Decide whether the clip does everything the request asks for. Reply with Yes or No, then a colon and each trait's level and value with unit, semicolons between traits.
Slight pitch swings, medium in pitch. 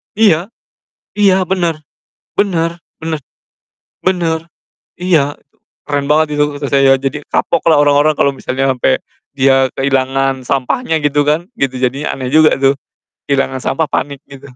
No: average, 3.0 semitones; medium, 145 Hz